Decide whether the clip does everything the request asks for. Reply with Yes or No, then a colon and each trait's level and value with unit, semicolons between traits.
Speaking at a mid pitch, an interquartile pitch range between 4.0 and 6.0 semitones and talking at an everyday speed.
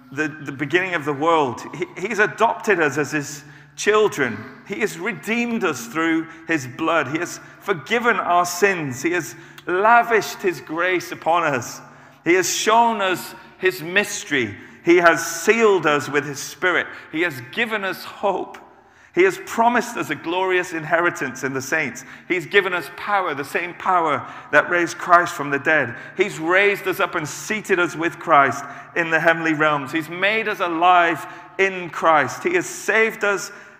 Yes: medium, 175 Hz; average, 4.5 semitones; average, 170 wpm